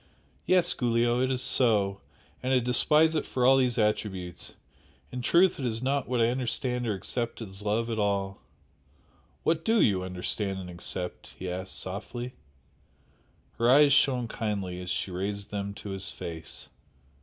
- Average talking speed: Yes, average, 165 wpm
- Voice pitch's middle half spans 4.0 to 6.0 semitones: Yes, average, 4.7 semitones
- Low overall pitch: Yes, low, 115 Hz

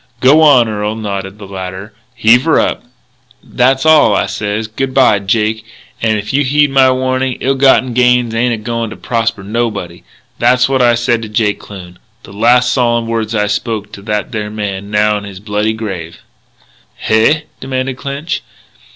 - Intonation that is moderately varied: Yes, average, 3.6 semitones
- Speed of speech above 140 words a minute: Yes, average, 175 wpm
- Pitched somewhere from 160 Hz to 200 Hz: No, low, 115 Hz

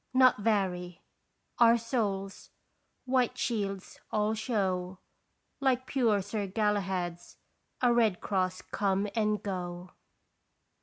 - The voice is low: No, high, 205 Hz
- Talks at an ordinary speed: No, slow, 105 wpm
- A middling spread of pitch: Yes, average, 3.6 semitones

